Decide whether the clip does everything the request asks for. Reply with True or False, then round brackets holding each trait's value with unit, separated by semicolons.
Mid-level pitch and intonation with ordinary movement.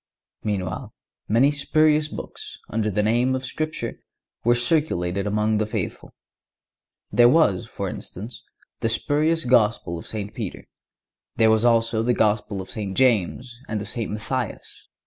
False (115 Hz; 3.5 semitones)